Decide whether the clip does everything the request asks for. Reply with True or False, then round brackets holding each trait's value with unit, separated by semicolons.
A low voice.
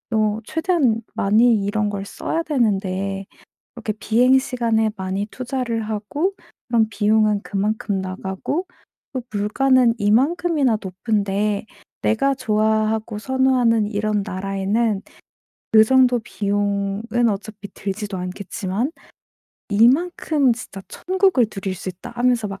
False (220 Hz)